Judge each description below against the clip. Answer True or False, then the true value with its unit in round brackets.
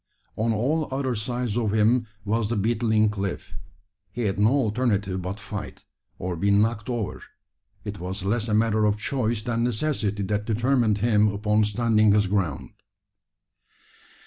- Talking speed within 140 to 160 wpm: True (150 wpm)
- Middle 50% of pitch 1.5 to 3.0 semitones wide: True (2.4 semitones)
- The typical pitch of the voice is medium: False (110 Hz)